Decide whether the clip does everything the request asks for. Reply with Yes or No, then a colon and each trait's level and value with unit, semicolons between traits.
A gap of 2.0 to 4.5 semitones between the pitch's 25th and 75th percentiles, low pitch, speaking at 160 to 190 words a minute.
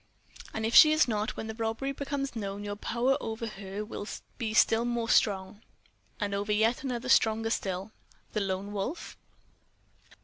No: average, 2.7 semitones; high, 220 Hz; average, 165 wpm